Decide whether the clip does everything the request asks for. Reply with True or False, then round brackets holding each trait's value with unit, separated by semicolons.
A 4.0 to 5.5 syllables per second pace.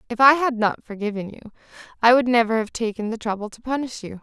False (6.2 syllables/s)